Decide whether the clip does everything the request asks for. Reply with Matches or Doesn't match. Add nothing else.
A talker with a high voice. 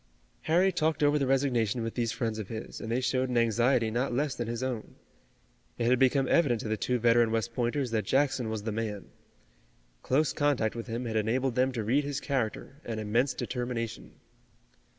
Doesn't match